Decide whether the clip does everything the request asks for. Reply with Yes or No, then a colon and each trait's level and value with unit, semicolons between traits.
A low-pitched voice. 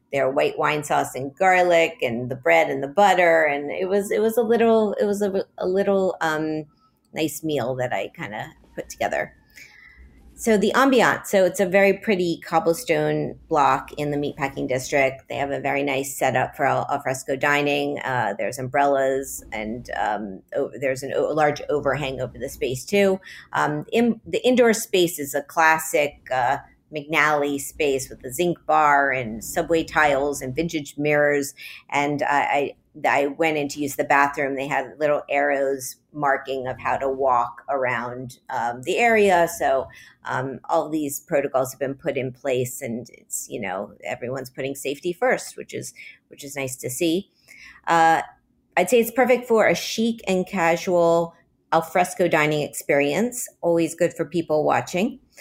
No: medium, 150 Hz